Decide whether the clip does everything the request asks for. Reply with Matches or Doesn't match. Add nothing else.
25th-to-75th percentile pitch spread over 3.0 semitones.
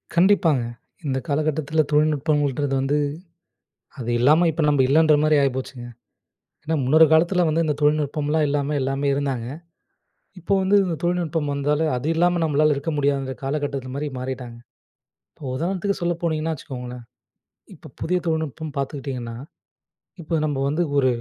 Doesn't match